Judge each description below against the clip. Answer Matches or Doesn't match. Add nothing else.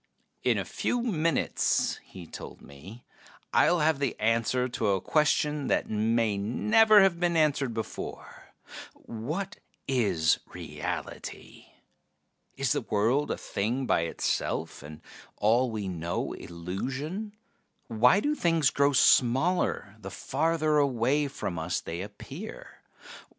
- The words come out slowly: Matches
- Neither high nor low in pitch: Doesn't match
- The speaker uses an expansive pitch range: Matches